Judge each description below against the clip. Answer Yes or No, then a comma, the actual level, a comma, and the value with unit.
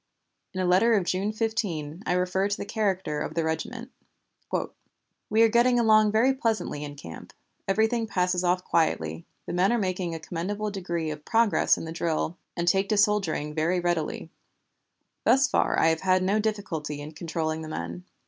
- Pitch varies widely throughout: No, average, 5.0 semitones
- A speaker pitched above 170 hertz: Yes, medium, 185 Hz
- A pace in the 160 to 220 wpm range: Yes, average, 180 wpm